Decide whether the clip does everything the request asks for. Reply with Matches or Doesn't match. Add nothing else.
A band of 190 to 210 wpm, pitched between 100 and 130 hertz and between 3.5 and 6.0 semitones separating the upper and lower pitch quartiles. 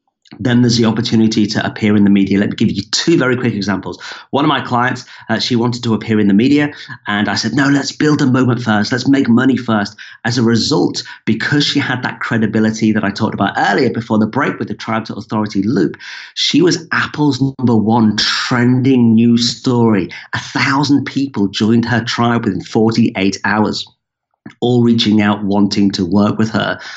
Doesn't match